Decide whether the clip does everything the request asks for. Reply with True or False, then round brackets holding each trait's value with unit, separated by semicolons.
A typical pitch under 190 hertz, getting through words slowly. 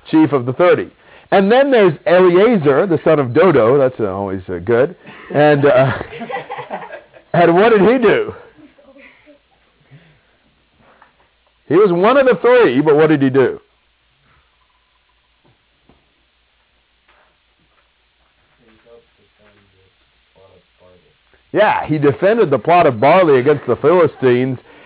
True (135 Hz; 110 wpm)